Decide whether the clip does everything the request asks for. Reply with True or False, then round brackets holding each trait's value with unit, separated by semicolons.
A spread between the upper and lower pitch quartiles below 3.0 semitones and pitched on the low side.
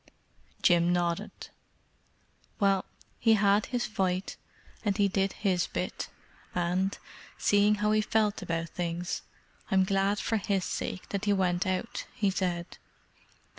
False (2.5 semitones; 195 Hz)